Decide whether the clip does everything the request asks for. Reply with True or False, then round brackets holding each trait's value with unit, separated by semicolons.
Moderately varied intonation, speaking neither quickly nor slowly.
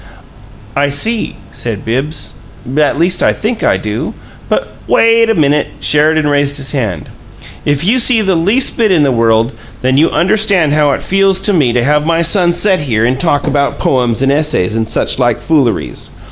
False (5.7 semitones; 190 wpm)